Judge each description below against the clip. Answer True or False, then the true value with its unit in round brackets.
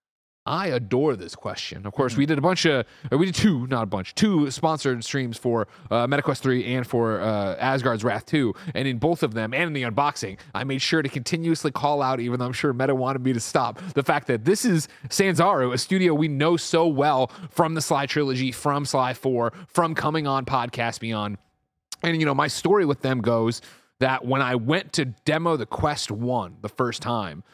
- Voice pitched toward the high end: False (135 Hz)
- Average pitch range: True (4.4 semitones)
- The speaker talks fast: True (215 wpm)